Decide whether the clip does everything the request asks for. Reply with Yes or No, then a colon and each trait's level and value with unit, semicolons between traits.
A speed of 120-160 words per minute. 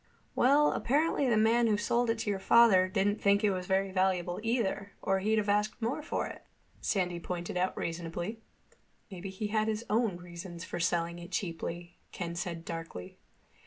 No: average, 180 wpm